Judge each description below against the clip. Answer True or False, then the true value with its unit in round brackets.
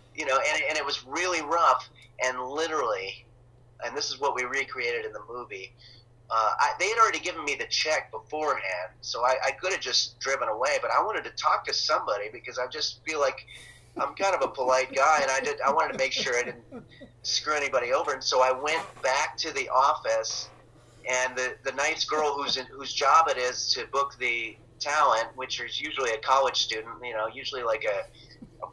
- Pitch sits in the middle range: False (130 Hz)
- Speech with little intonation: False (3.9 semitones)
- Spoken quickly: True (215 wpm)